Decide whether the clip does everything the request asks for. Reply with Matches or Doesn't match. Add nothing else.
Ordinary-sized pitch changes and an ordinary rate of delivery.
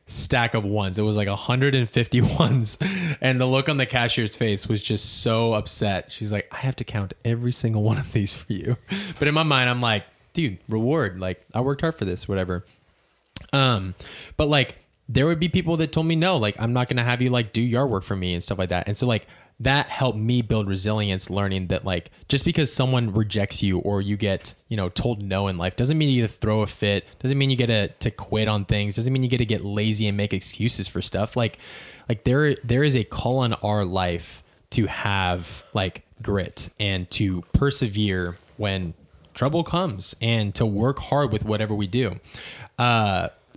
Doesn't match